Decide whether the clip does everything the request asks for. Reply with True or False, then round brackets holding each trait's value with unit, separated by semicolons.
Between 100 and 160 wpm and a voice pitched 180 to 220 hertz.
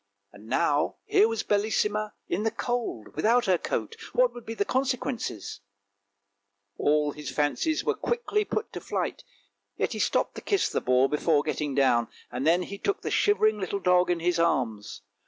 False (175 wpm; 185 Hz)